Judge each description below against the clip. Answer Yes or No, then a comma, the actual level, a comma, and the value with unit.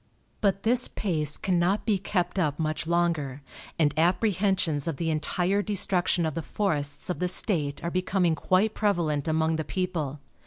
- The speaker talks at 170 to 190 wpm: No, average, 160 wpm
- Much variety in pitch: No, average, 3.7 semitones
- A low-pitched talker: No, medium, 175 Hz